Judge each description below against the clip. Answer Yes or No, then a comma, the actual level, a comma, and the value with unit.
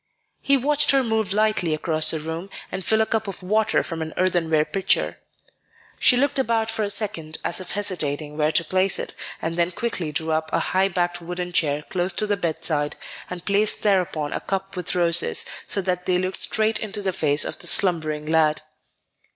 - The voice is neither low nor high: Yes, medium, 180 Hz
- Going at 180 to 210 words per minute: Yes, average, 200 wpm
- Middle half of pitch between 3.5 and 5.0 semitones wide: Yes, average, 4.4 semitones